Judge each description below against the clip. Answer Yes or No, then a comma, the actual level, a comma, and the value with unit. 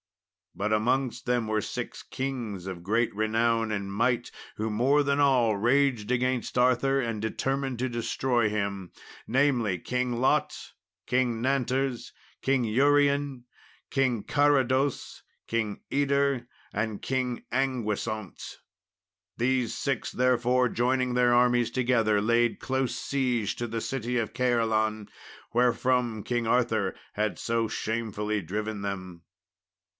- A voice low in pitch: Yes, low, 120 Hz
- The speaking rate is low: Yes, slow, 120 wpm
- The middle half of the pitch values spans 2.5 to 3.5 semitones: Yes, average, 3.0 semitones